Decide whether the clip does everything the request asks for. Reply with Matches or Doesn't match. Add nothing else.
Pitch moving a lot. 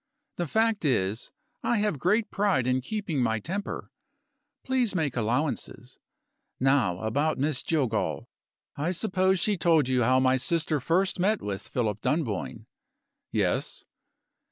Matches